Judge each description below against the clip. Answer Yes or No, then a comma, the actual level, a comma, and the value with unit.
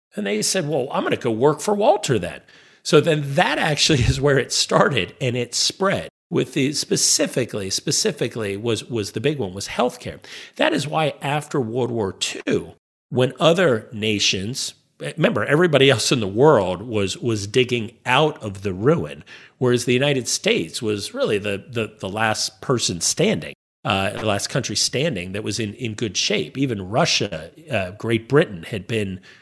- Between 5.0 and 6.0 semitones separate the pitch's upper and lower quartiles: Yes, average, 5.3 semitones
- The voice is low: Yes, low, 120 Hz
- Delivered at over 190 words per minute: No, average, 175 wpm